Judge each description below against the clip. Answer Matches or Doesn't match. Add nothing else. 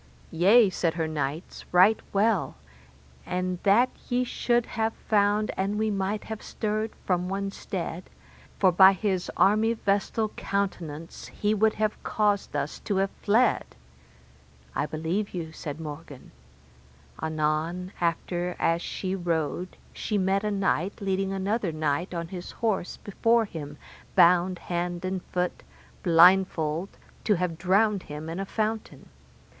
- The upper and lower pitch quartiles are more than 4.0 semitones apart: Doesn't match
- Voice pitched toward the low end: Doesn't match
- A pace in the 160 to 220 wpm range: Doesn't match